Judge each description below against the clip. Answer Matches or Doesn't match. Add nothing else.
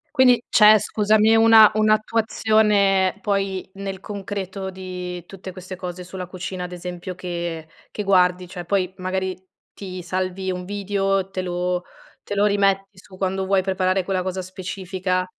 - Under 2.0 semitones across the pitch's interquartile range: Matches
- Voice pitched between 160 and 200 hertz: Matches